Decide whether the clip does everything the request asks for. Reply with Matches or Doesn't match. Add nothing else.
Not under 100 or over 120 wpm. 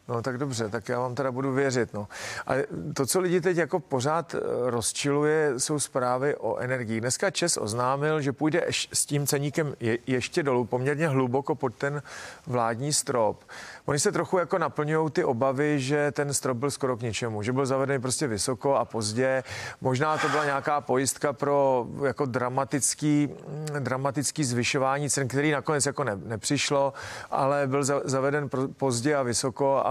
Doesn't match